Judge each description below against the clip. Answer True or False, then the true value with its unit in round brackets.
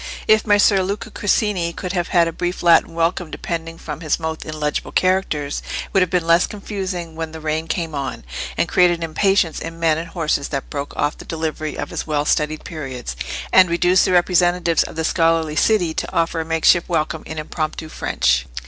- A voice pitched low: False (165 Hz)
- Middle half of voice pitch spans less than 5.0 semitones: True (2.4 semitones)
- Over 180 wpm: True (200 wpm)